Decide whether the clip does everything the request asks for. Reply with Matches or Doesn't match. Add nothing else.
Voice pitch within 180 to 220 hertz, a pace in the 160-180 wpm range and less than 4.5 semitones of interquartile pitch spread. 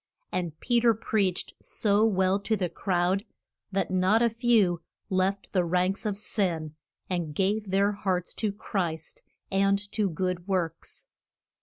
Doesn't match